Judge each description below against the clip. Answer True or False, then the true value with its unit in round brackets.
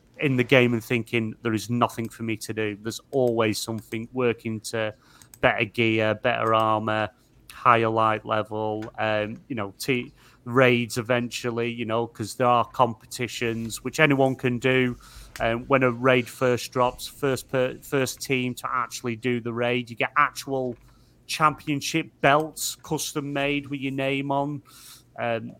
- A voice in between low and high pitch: False (120 Hz)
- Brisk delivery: False (160 wpm)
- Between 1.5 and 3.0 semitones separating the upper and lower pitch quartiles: True (2.5 semitones)